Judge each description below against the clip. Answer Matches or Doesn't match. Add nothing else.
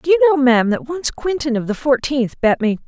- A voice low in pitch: Doesn't match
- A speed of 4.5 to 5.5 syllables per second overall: Doesn't match